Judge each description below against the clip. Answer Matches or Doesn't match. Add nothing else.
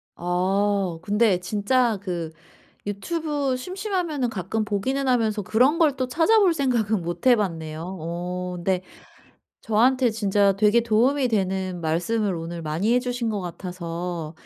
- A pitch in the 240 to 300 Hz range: Doesn't match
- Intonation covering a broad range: Matches